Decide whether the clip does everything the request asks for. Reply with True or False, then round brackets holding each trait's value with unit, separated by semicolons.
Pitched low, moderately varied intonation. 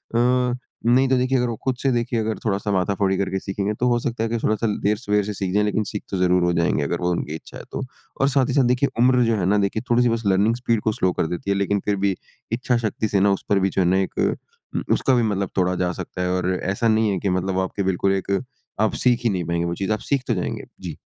True (105 Hz; 3.8 semitones)